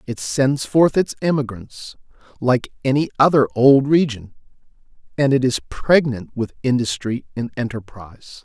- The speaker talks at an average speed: No, slow, 130 wpm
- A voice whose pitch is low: Yes, low, 130 Hz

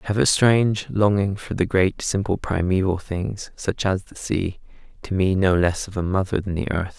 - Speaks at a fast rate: Yes, fast, 215 wpm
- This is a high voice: No, very low, 95 Hz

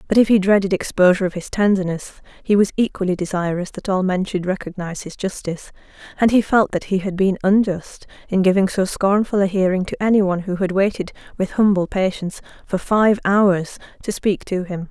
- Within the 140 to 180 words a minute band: No, average, 195 wpm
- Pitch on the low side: No, high, 190 Hz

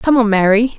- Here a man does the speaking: No, female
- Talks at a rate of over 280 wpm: No, fast, 230 wpm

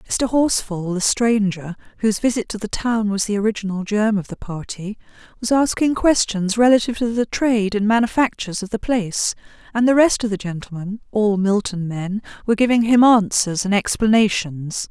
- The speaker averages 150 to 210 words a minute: Yes, average, 165 wpm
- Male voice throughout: No, female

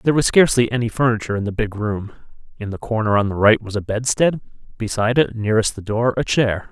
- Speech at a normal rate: No, fast, 225 wpm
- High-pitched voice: No, low, 110 Hz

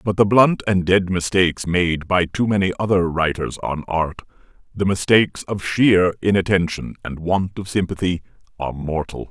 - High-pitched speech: No, very low, 90 Hz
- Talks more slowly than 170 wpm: Yes, average, 150 wpm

